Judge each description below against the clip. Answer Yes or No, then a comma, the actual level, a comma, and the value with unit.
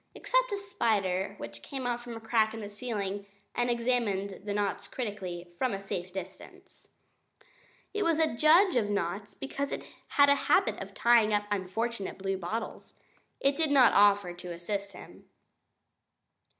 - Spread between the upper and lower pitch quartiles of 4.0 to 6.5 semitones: Yes, average, 4.3 semitones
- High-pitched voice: Yes, high, 210 Hz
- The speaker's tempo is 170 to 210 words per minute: No, average, 160 wpm